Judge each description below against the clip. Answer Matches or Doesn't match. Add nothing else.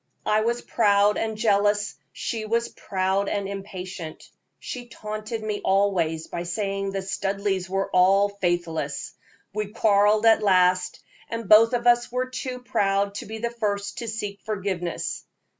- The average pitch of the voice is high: Matches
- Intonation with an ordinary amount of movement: Doesn't match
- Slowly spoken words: Doesn't match